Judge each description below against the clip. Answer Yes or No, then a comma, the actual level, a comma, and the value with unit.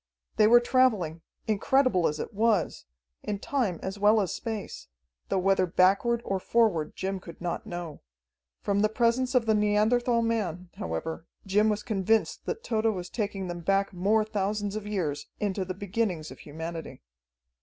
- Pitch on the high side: Yes, high, 200 Hz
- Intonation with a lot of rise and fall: No, average, 3.5 semitones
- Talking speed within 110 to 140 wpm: No, average, 165 wpm